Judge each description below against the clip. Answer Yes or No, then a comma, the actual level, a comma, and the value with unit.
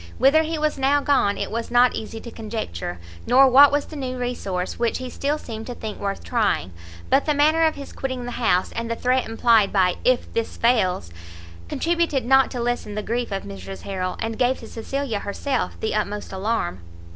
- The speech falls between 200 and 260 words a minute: Yes, fast, 205 wpm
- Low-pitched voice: No, high, 240 Hz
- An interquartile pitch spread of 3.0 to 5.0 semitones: Yes, average, 4.3 semitones